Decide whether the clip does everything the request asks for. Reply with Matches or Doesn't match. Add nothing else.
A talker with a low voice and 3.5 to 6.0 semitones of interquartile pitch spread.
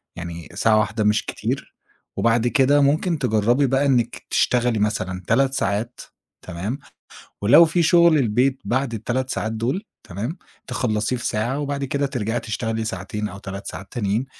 Matches